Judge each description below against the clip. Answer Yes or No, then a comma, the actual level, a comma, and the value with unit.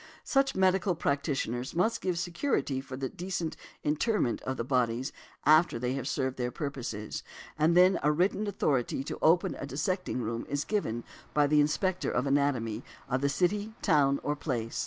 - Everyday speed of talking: Yes, average, 170 wpm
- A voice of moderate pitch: Yes, medium, 145 Hz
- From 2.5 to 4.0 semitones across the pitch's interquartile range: No, wide, 5.6 semitones